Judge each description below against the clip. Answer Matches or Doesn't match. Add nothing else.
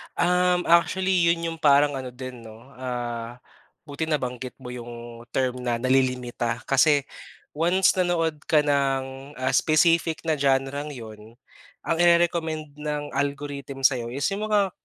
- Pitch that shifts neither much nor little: Matches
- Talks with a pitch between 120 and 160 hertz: Matches